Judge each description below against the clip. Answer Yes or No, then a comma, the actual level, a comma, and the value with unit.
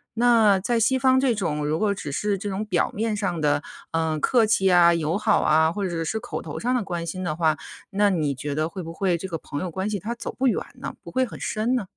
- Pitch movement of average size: Yes, average, 5.0 semitones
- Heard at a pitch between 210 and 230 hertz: No, high, 190 Hz